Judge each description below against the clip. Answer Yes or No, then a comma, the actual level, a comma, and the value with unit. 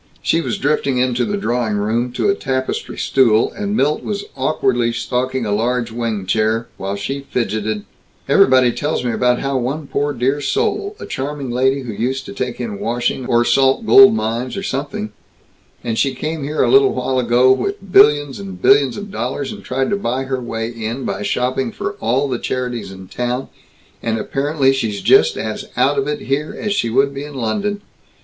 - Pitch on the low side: Yes, low, 130 Hz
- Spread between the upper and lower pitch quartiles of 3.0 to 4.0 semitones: Yes, average, 3.7 semitones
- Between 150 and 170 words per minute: No, average, 195 wpm